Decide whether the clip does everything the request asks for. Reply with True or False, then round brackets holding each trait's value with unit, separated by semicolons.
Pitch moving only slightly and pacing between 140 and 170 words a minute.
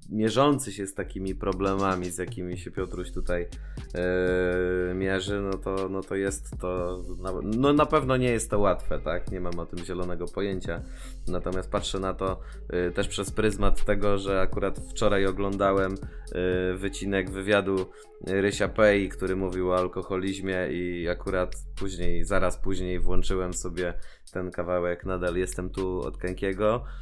True (1.6 semitones; 155 wpm)